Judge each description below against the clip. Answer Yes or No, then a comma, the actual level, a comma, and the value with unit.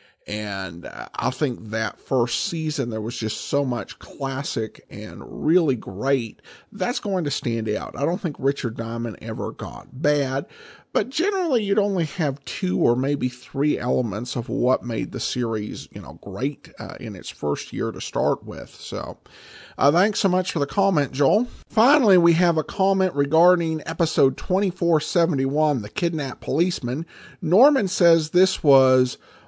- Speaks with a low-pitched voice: No, medium, 145 Hz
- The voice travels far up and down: Yes, wide, 6.4 semitones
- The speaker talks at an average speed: Yes, average, 165 wpm